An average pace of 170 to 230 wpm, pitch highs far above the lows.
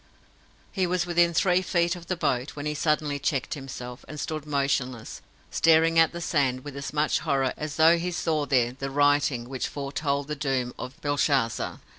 No: average, 185 wpm; average, 3.2 semitones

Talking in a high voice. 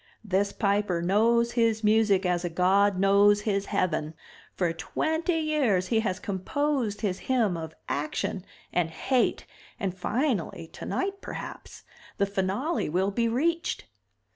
Yes: high, 200 Hz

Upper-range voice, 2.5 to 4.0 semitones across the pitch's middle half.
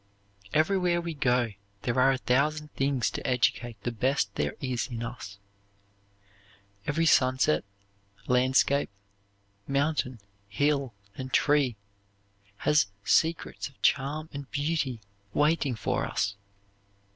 No: low, 135 Hz; average, 3.3 semitones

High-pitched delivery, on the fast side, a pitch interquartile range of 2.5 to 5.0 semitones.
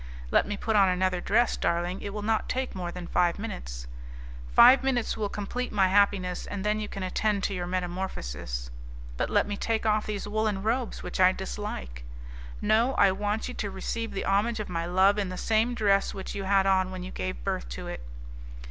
Yes: high, 195 Hz; fast, 210 wpm; average, 2.8 semitones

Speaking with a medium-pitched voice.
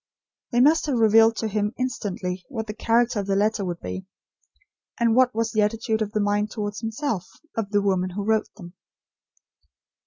No: high, 215 Hz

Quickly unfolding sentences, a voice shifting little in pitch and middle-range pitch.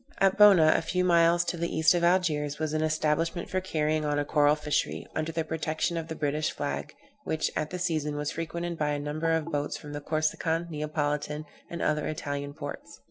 Yes: fast, 210 wpm; narrow, 2.0 semitones; medium, 155 Hz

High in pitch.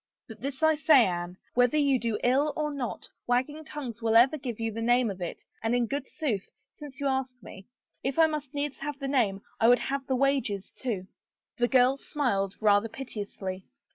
Yes: very high, 250 Hz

